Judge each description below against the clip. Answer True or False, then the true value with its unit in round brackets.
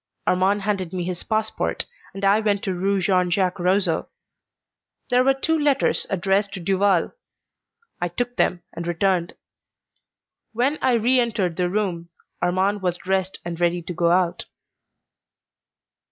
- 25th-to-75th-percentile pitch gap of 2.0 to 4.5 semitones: True (2.9 semitones)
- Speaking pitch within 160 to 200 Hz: True (190 Hz)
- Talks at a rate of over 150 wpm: False (145 wpm)